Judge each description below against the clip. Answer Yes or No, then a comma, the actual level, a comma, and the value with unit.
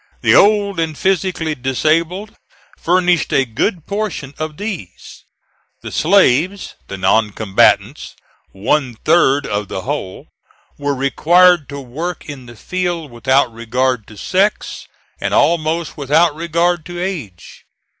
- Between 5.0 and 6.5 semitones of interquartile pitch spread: Yes, wide, 5.6 semitones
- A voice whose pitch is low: No, medium, 155 Hz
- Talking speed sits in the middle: No, slow, 125 wpm